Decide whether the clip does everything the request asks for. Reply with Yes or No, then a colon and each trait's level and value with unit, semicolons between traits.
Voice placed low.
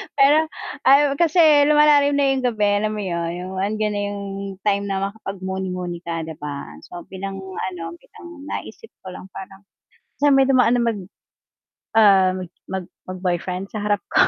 No: high, 200 Hz